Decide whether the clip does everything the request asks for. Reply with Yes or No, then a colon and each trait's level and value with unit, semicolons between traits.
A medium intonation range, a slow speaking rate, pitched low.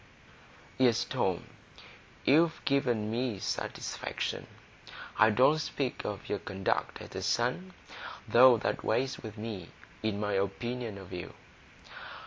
Yes: average, 3.9 semitones; slow, 120 wpm; low, 115 Hz